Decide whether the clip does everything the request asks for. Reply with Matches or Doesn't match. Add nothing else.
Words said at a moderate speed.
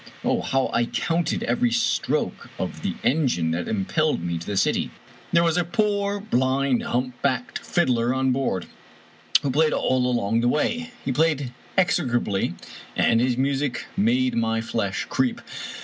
Matches